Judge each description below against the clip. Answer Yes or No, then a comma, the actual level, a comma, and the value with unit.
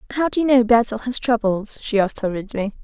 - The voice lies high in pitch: Yes, high, 230 Hz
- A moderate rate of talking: No, fast, 210 wpm